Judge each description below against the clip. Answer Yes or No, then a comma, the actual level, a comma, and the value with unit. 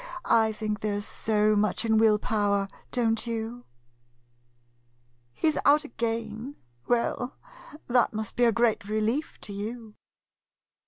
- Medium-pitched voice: No, high, 225 Hz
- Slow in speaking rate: Yes, slow, 130 wpm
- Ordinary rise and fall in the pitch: No, narrow, 2.1 semitones